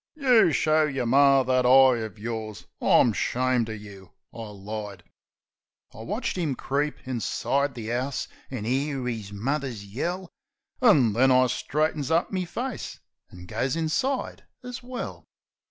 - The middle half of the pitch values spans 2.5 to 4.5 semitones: No, wide, 5.6 semitones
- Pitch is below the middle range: Yes, low, 130 Hz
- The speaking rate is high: No, average, 145 wpm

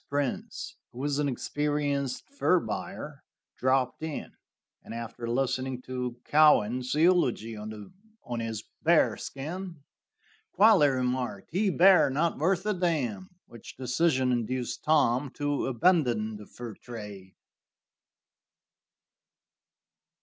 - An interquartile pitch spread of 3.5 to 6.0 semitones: Yes, average, 4.8 semitones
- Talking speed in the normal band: No, slow, 110 wpm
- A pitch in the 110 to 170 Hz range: Yes, low, 135 Hz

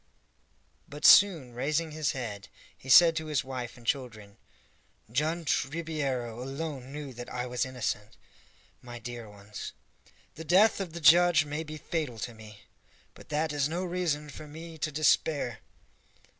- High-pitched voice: No, medium, 145 Hz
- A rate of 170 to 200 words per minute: No, average, 155 wpm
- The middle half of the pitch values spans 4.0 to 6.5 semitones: Yes, average, 4.6 semitones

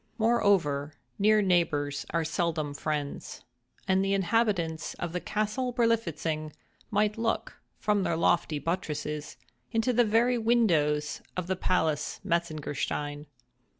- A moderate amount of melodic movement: No, wide, 5.8 semitones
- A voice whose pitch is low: No, medium, 175 Hz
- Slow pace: Yes, slow, 115 wpm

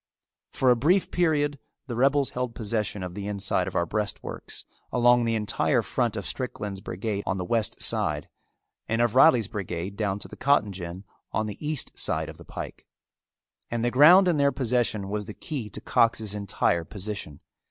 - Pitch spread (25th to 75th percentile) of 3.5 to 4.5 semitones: Yes, average, 4.1 semitones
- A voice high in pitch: No, low, 110 Hz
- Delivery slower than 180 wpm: No, average, 185 wpm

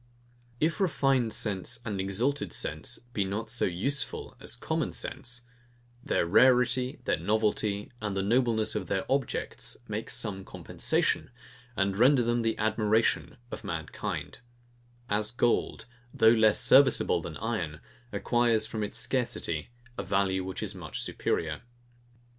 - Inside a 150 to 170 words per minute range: No, slow, 135 wpm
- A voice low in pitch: Yes, low, 110 Hz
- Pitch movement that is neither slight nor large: Yes, average, 3.6 semitones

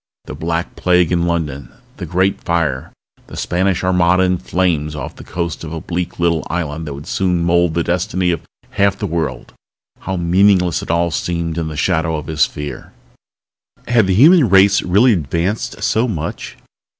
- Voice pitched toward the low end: Yes, very low, 85 Hz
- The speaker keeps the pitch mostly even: Yes, narrow, 2.3 semitones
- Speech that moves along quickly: No, average, 175 wpm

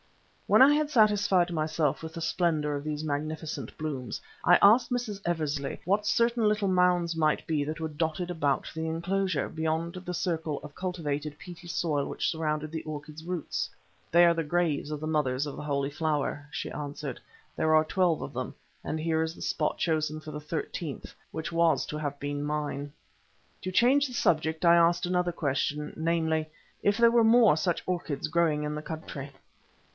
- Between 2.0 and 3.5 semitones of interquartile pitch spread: Yes, average, 2.8 semitones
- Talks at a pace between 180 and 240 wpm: Yes, average, 185 wpm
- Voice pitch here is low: No, medium, 160 Hz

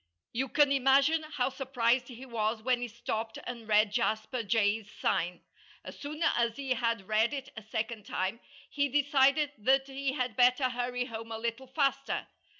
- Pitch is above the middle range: Yes, high, 245 Hz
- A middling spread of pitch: Yes, average, 3.3 semitones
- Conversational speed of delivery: Yes, average, 170 wpm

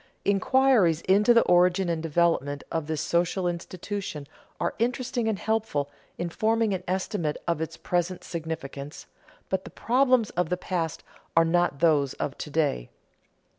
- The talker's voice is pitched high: No, medium, 175 Hz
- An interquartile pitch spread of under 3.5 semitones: No, average, 4.2 semitones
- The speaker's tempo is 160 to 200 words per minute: No, average, 150 wpm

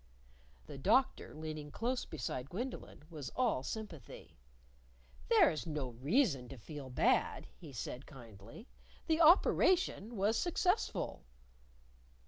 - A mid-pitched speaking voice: Yes, medium, 155 Hz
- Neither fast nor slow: No, slow, 110 wpm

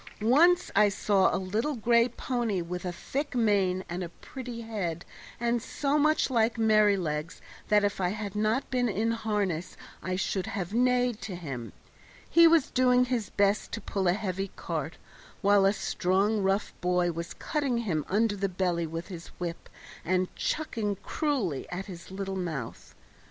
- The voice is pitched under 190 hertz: No, high, 205 Hz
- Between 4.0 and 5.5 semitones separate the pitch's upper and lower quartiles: Yes, average, 4.4 semitones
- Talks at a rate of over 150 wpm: Yes, average, 165 wpm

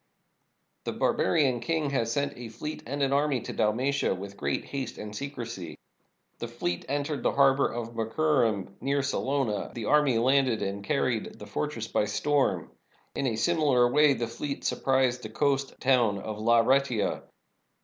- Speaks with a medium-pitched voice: No, low, 130 Hz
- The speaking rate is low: No, average, 165 wpm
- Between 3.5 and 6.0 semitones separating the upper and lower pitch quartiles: Yes, average, 3.9 semitones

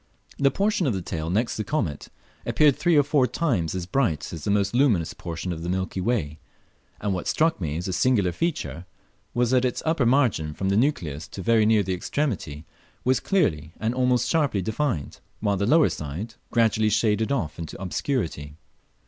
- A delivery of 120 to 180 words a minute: No, average, 190 wpm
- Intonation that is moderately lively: No, wide, 7.1 semitones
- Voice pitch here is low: Yes, low, 105 Hz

